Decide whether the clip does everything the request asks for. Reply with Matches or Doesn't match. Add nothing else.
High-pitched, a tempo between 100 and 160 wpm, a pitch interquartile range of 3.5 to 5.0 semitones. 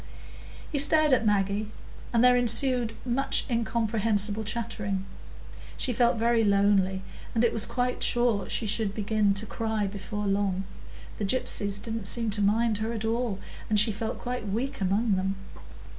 Doesn't match